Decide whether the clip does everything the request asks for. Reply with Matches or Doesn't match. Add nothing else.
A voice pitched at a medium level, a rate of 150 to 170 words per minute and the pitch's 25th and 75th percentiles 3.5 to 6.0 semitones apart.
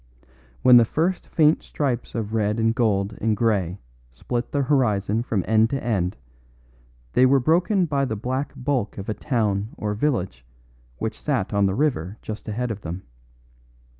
Doesn't match